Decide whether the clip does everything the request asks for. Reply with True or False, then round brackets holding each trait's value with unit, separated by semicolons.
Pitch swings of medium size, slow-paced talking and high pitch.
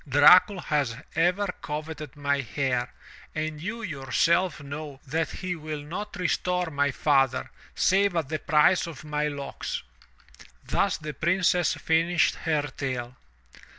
False (3.7 semitones; 130 wpm; 155 Hz)